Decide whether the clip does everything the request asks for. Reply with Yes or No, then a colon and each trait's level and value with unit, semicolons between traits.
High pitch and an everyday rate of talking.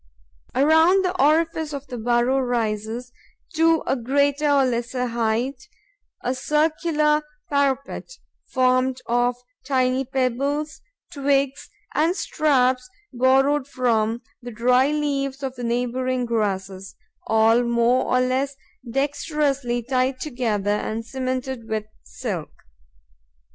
No: very high, 255 Hz; slow, 110 wpm